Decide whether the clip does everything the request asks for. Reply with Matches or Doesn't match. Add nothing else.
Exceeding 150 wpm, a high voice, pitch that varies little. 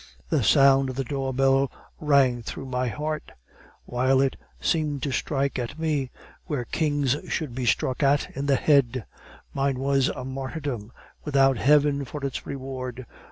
Doesn't match